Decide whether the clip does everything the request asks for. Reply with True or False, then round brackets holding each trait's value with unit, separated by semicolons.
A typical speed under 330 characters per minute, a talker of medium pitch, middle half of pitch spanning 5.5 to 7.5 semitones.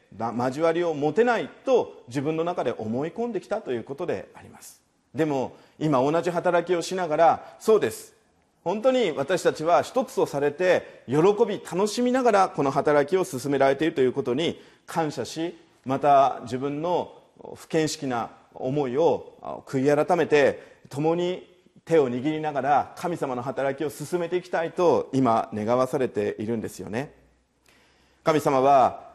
True (305 characters per minute; 165 Hz; 5.8 semitones)